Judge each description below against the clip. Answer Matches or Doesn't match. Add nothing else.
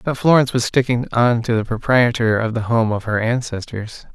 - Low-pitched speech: Matches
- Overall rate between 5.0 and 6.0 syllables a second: Matches